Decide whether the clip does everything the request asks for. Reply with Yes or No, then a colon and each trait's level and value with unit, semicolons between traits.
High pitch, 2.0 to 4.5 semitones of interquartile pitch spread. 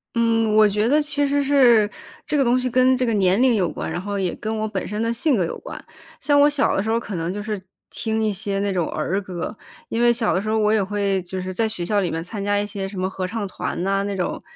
Yes: high, 210 Hz; average, 3.3 semitones